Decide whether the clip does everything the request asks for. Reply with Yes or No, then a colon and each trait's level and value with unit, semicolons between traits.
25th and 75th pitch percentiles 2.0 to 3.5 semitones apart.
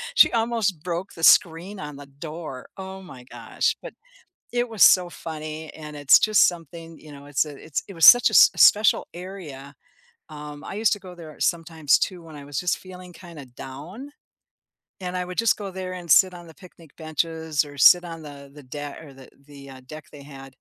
No: average, 3.9 semitones